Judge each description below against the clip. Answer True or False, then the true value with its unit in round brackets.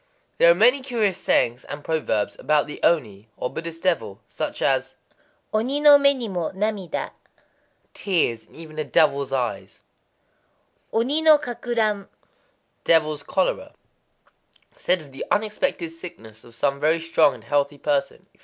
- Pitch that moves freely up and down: True (7.3 semitones)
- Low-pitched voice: False (165 Hz)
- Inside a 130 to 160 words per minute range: True (140 wpm)